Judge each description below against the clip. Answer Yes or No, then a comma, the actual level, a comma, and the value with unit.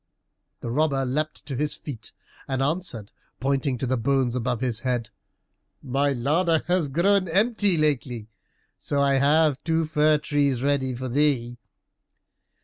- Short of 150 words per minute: Yes, average, 140 wpm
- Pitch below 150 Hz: Yes, medium, 140 Hz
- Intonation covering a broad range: No, average, 3.4 semitones